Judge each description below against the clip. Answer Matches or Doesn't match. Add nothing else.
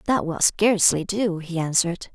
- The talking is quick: Doesn't match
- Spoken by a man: Doesn't match